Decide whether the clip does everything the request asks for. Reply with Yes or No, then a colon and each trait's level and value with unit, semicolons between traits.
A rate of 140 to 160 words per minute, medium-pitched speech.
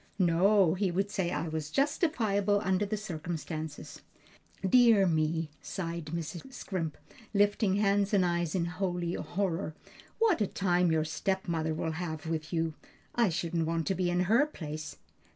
Yes: average, 150 wpm; medium, 175 Hz